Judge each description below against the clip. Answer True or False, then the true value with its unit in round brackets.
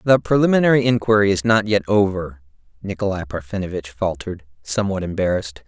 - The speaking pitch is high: False (100 Hz)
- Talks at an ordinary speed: False (125 wpm)